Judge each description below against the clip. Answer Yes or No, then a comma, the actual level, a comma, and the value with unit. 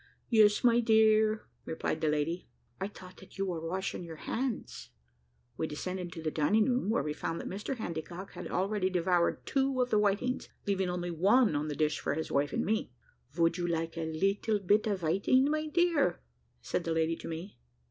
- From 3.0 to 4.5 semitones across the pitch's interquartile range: No, average, 4.9 semitones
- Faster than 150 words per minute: Yes, average, 200 wpm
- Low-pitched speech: No, medium, 185 Hz